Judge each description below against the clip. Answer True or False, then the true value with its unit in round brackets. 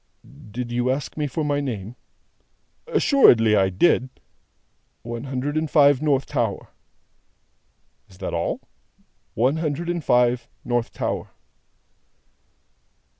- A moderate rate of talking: False (115 wpm)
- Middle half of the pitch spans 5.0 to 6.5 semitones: False (3.7 semitones)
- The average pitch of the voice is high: False (130 Hz)